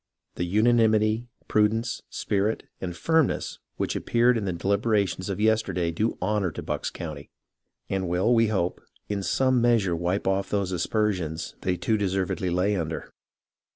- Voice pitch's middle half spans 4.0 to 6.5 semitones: No, average, 3.4 semitones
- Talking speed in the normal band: Yes, average, 150 wpm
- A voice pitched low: Yes, low, 100 Hz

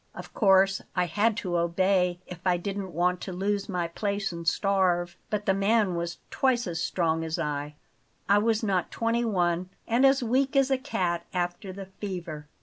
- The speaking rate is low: No, average, 185 wpm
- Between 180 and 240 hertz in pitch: Yes, high, 190 Hz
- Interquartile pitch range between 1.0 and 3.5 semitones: Yes, average, 3.0 semitones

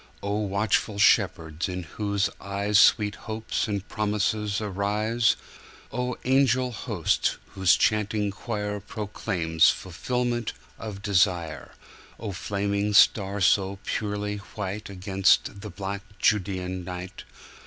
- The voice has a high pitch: No, low, 100 Hz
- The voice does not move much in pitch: Yes, narrow, 1.9 semitones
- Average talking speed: No, slow, 90 wpm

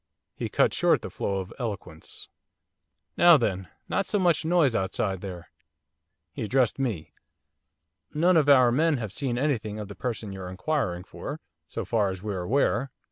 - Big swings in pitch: Yes, wide, 6.9 semitones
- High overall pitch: No, low, 115 Hz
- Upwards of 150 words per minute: Yes, average, 165 wpm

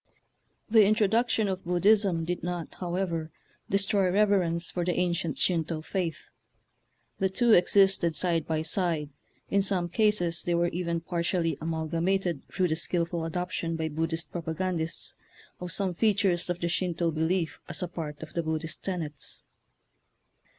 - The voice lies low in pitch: No, medium, 175 Hz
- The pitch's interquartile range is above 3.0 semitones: No, narrow, 2.5 semitones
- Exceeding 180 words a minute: No, average, 140 wpm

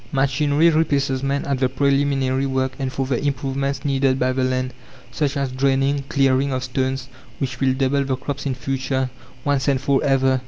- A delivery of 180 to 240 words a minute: Yes, average, 185 wpm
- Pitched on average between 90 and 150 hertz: Yes, low, 135 Hz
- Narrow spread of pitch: Yes, narrow, 1.1 semitones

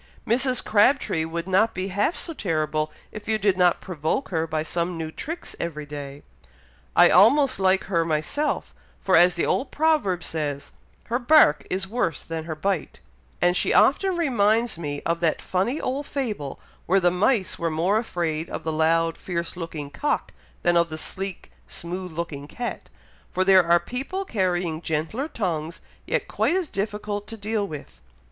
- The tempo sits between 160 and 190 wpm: Yes, average, 170 wpm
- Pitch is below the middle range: No, medium, 180 Hz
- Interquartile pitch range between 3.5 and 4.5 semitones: No, average, 5.3 semitones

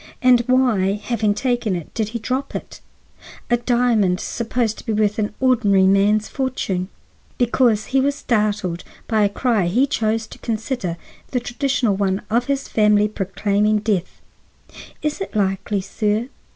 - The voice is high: Yes, high, 215 Hz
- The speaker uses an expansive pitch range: No, average, 3.3 semitones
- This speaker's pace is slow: No, average, 150 wpm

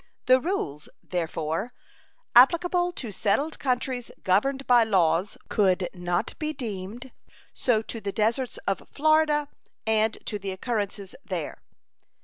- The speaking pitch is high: Yes, high, 220 Hz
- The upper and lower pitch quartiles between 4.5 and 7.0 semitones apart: Yes, wide, 5.5 semitones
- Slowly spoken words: Yes, slow, 125 wpm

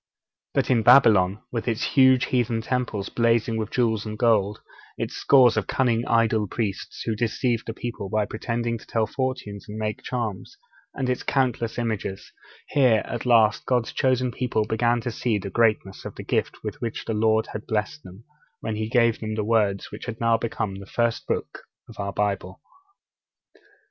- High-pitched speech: No, low, 115 Hz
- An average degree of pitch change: No, narrow, 2.1 semitones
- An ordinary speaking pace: Yes, average, 180 wpm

